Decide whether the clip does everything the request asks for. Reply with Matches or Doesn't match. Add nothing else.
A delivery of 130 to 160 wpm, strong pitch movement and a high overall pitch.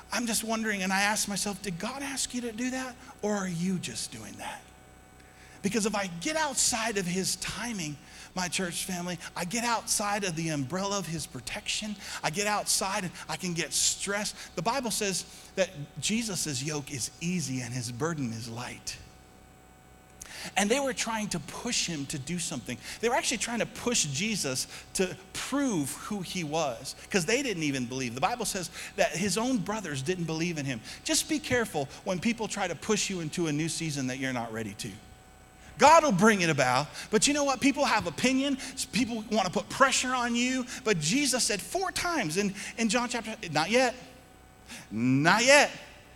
Doesn't match